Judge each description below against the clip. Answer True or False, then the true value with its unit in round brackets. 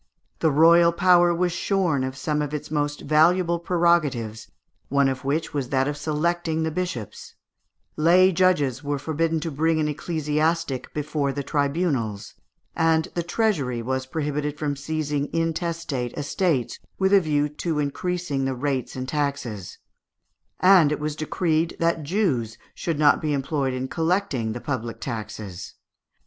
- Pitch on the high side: False (150 Hz)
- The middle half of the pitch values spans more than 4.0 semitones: False (3.4 semitones)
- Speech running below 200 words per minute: True (150 wpm)